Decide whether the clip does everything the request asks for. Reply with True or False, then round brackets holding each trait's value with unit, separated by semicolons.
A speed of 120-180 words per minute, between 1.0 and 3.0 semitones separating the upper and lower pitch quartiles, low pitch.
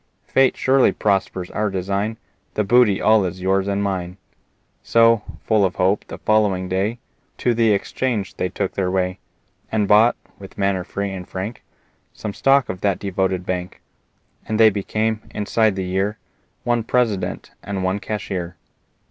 True (155 wpm; 2.6 semitones; 100 Hz)